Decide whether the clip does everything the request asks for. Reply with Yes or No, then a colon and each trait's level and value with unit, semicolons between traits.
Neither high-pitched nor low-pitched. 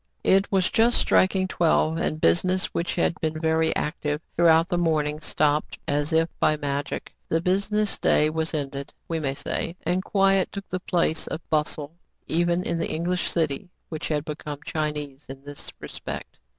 Yes: medium, 160 Hz